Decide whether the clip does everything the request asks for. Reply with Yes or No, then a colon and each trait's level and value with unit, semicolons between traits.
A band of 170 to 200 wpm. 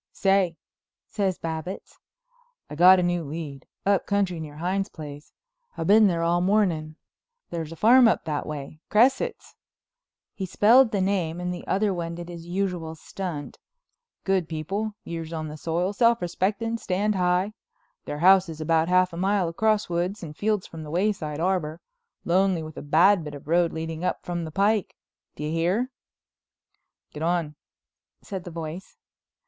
No: average, 160 wpm